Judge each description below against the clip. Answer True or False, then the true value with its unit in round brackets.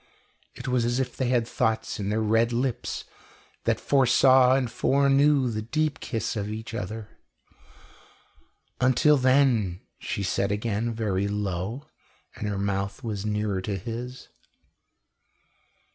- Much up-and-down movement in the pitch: False (3.8 semitones)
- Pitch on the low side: True (115 Hz)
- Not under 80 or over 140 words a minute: True (135 wpm)